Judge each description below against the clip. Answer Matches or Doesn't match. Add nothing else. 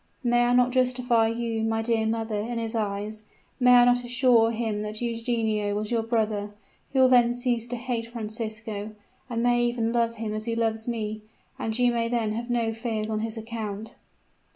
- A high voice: Matches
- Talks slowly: Doesn't match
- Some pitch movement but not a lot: Doesn't match